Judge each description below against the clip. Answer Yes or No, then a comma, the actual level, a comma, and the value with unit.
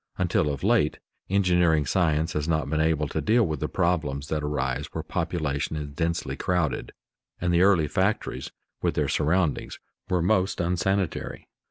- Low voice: Yes, very low, 80 Hz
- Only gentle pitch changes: No, average, 3.1 semitones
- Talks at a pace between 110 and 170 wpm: Yes, average, 160 wpm